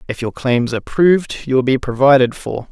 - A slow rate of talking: No, fast, 220 wpm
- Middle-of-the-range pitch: No, low, 130 Hz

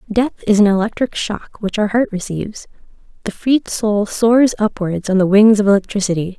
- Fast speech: No, average, 180 wpm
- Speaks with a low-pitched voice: No, high, 210 Hz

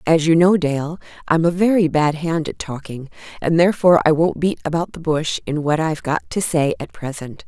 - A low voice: No, medium, 160 Hz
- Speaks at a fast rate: Yes, fast, 215 wpm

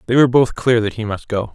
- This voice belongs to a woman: No, male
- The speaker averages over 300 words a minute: Yes, fast, 310 wpm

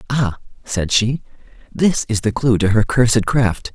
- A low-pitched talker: Yes, low, 115 Hz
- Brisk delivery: No, average, 175 wpm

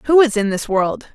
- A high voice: Yes, high, 230 Hz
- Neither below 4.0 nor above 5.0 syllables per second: Yes, 4.7 syllables/s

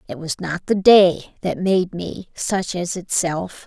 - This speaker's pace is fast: No, average, 180 wpm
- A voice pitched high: No, medium, 175 Hz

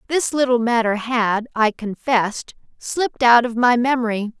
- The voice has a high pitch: Yes, high, 240 Hz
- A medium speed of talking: Yes, average, 150 wpm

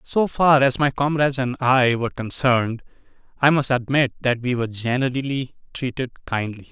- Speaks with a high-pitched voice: No, low, 130 Hz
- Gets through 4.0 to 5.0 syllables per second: No, 5.2 syllables/s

